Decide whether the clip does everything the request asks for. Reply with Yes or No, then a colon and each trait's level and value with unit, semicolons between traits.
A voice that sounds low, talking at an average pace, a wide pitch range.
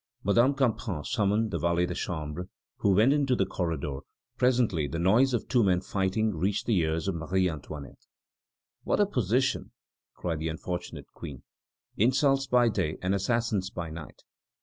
Yes: very low, 95 Hz; average, 160 wpm; wide, 6.1 semitones